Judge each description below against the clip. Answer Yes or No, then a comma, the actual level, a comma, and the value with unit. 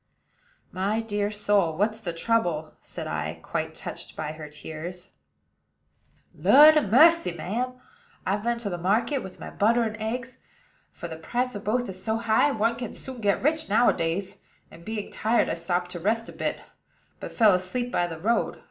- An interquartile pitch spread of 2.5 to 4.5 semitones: No, average, 5.0 semitones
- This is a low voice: No, high, 210 Hz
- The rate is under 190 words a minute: Yes, average, 175 wpm